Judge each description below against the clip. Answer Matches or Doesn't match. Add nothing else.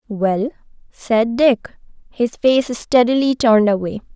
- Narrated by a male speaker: Doesn't match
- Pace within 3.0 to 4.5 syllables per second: Matches